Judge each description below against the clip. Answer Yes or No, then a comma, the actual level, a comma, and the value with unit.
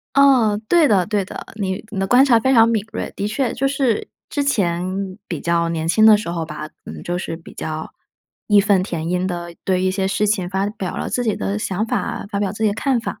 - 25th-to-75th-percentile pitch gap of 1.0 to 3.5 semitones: No, average, 3.9 semitones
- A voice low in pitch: No, high, 200 Hz